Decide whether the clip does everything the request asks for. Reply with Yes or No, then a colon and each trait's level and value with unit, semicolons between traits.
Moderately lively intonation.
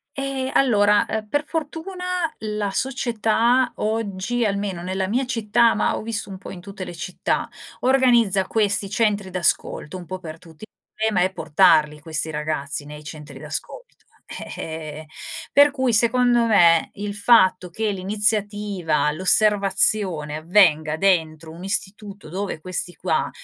Yes: average, 4.8 semitones